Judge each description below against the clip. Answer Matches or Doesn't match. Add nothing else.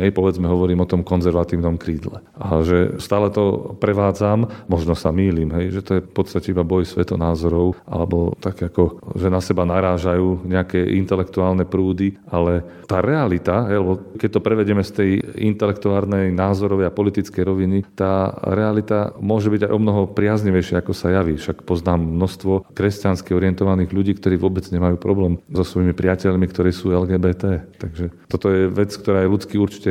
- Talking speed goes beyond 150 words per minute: Matches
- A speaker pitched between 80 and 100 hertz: Matches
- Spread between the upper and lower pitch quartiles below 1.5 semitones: Doesn't match